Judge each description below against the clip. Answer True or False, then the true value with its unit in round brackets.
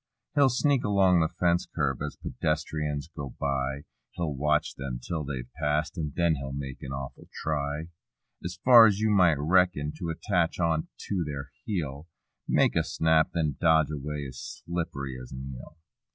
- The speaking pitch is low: True (75 Hz)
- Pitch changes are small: False (3.7 semitones)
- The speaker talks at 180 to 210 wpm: False (170 wpm)